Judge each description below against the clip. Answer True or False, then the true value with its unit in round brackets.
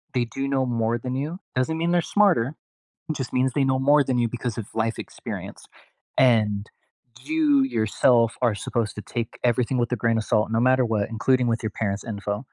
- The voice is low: True (120 Hz)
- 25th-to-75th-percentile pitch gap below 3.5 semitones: True (3.0 semitones)